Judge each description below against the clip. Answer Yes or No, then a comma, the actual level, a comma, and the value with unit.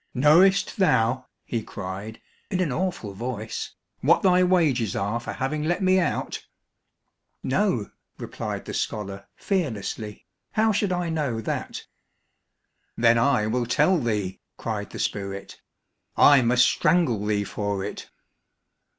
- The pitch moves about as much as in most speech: No, wide, 8.7 semitones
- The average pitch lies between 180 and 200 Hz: No, low, 125 Hz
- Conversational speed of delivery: No, slow, 130 wpm